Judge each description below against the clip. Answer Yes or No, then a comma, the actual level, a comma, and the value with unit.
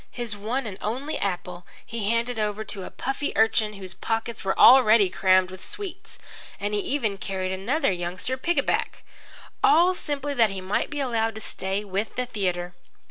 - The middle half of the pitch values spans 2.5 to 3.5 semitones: No, average, 4.7 semitones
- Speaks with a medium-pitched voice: No, high, 215 Hz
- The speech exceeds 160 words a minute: Yes, average, 175 wpm